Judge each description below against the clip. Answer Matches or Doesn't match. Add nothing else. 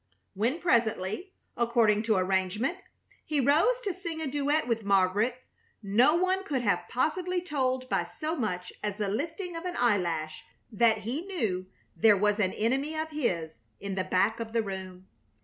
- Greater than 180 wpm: Doesn't match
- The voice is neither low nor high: Doesn't match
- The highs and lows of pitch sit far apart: Matches